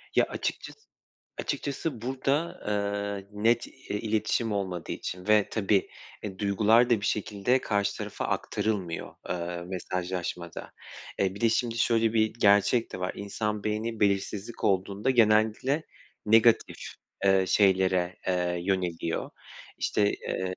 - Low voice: Yes, low, 105 Hz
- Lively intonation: No, average, 3.1 semitones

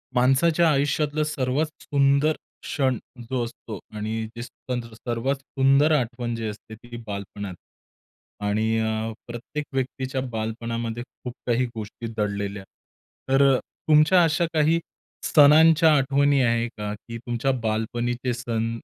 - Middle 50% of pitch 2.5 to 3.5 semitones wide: No, average, 3.9 semitones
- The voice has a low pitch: Yes, low, 125 Hz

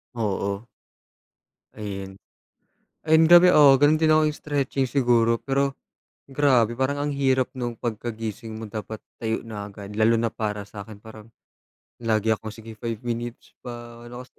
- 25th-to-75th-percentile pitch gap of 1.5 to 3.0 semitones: No, average, 3.5 semitones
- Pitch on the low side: Yes, low, 115 Hz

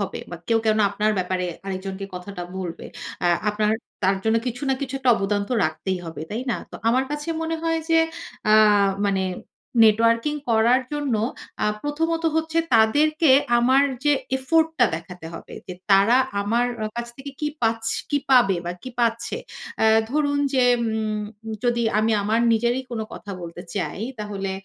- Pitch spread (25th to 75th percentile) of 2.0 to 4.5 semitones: No, average, 5.1 semitones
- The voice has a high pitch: Yes, high, 225 Hz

